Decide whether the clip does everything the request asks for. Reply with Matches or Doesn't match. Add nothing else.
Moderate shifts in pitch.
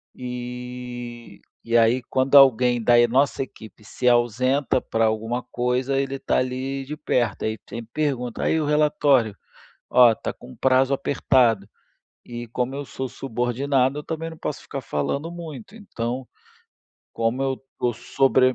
Doesn't match